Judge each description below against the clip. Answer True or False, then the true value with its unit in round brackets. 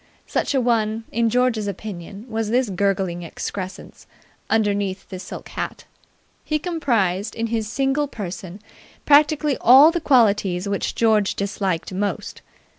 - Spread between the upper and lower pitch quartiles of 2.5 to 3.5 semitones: False (4.2 semitones)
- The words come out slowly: True (130 wpm)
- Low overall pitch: False (215 Hz)